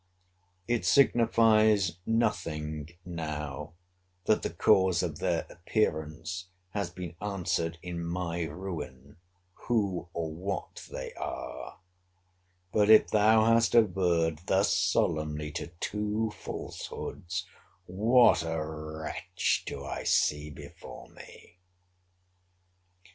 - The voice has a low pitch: Yes, very low, 90 Hz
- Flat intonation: No, average, 4.6 semitones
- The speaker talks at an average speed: No, slow, 100 wpm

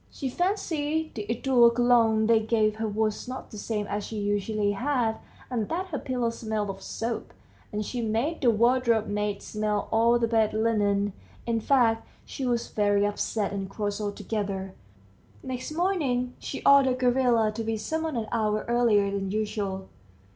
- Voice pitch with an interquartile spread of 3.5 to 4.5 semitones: No, average, 3.1 semitones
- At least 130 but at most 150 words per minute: No, average, 170 wpm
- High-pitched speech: Yes, high, 225 Hz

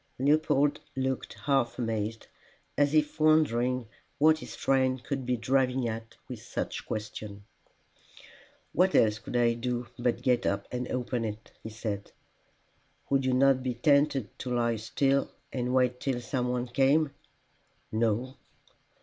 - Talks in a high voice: No, low, 125 Hz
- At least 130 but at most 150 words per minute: Yes, average, 145 wpm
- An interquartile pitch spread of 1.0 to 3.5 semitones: Yes, average, 2.7 semitones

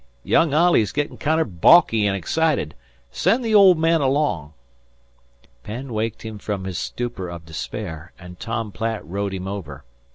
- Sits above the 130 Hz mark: No, low, 110 Hz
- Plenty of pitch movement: Yes, wide, 8.5 semitones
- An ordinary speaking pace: Yes, average, 155 wpm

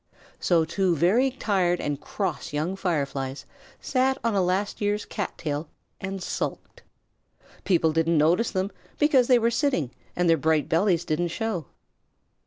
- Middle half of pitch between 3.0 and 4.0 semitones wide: No, average, 4.6 semitones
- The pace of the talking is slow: No, average, 150 wpm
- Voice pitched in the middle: Yes, medium, 180 Hz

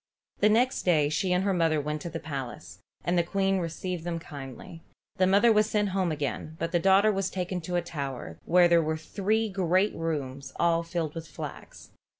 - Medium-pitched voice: Yes, medium, 170 Hz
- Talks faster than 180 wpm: Yes, average, 200 wpm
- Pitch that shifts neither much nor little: Yes, average, 3.5 semitones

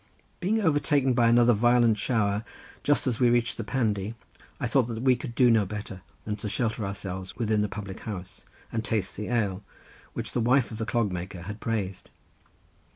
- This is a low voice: Yes, low, 110 Hz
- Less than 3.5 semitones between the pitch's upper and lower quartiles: Yes, average, 2.9 semitones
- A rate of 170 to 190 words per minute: Yes, average, 185 wpm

